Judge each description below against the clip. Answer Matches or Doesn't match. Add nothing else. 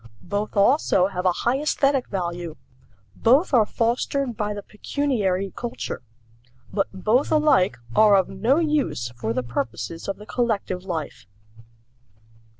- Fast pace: Doesn't match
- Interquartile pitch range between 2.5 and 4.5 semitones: Doesn't match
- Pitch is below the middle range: Doesn't match